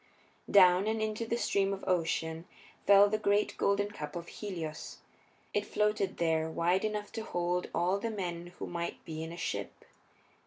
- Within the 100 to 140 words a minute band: No, average, 170 wpm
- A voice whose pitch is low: No, high, 190 Hz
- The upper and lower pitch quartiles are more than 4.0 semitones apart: No, average, 3.4 semitones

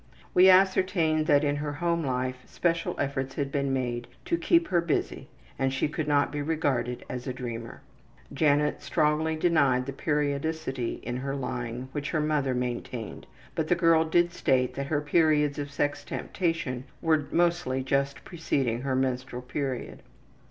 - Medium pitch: Yes, medium, 145 Hz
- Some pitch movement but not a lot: Yes, average, 3.6 semitones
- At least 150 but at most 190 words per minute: Yes, average, 160 wpm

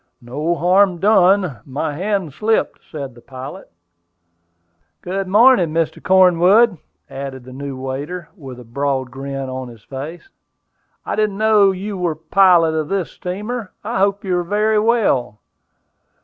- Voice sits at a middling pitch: Yes, medium, 175 Hz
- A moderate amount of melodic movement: No, wide, 6.4 semitones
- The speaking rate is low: No, average, 150 wpm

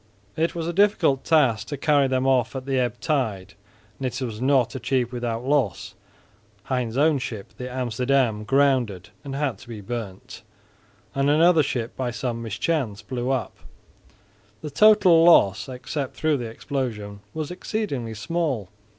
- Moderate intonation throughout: Yes, average, 3.9 semitones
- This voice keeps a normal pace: Yes, average, 155 wpm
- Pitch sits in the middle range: No, low, 130 Hz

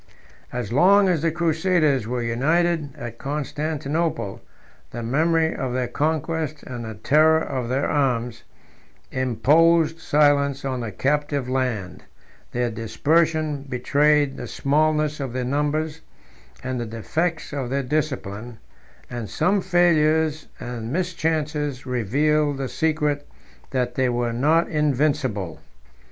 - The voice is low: No, medium, 145 Hz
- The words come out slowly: Yes, slow, 120 wpm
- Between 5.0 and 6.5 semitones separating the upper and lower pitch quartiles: No, average, 4.0 semitones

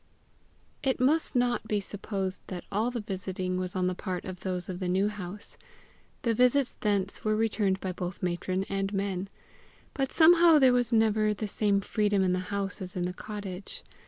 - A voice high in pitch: Yes, high, 200 Hz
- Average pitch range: Yes, average, 3.1 semitones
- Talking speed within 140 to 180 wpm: No, average, 190 wpm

